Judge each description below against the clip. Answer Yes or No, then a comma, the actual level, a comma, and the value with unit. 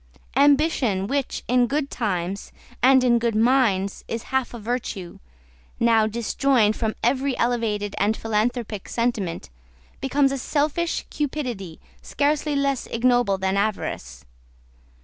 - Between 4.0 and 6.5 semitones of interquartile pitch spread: Yes, average, 4.5 semitones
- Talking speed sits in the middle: No, slow, 120 wpm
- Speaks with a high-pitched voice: Yes, high, 235 Hz